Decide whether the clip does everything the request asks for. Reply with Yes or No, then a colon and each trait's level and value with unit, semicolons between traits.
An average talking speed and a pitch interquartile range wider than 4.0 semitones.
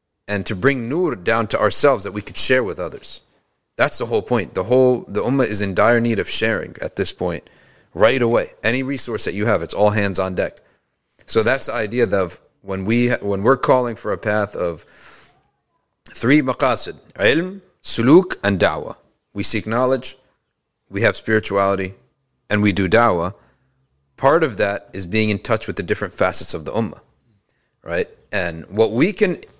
Yes: average, 185 wpm; average, 4.4 semitones